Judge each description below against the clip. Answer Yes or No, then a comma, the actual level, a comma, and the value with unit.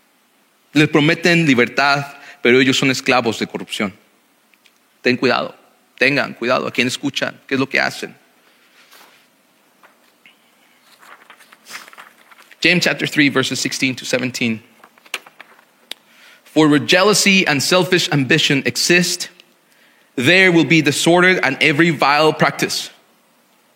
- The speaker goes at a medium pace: No, slow, 110 wpm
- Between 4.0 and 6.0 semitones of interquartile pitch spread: Yes, average, 4.4 semitones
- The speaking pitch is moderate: Yes, medium, 150 Hz